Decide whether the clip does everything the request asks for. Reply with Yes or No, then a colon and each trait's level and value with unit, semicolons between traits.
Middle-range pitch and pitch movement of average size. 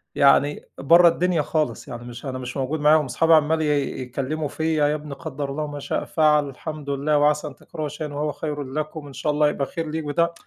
No: medium, 150 Hz; narrow, 1.8 semitones